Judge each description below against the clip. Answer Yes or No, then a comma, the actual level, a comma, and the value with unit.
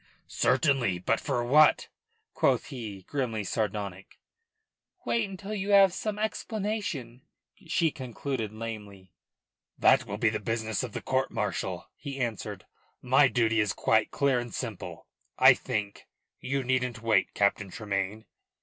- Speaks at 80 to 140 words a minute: Yes, slow, 135 wpm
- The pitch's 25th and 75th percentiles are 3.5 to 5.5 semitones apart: Yes, average, 4.8 semitones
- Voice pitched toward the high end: No, low, 120 Hz